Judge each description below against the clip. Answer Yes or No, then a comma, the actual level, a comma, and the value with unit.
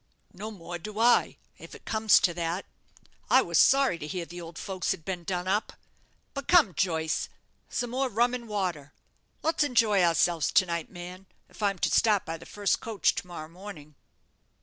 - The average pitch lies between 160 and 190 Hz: Yes, medium, 185 Hz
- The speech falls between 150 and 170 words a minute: No, average, 190 wpm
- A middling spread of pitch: Yes, average, 4.3 semitones